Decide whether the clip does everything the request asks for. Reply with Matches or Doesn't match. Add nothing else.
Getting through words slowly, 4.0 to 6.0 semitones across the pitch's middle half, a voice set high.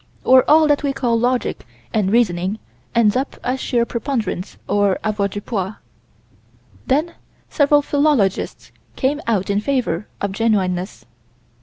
Matches